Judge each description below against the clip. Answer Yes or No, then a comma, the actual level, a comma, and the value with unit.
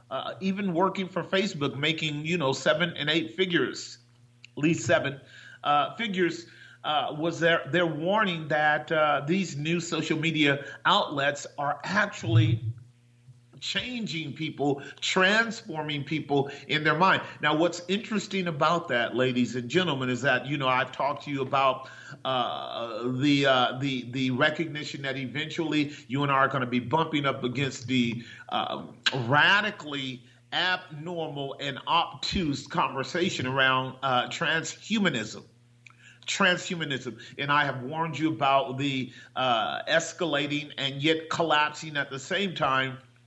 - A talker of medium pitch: Yes, medium, 145 Hz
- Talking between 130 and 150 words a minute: Yes, average, 140 wpm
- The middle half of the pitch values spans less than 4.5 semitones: Yes, average, 4.1 semitones